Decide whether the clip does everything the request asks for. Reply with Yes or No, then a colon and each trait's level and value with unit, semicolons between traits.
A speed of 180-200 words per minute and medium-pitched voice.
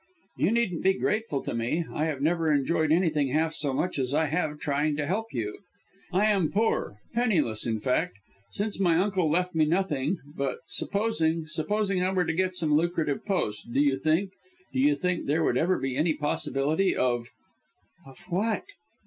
Yes: average, 185 wpm; medium, 160 Hz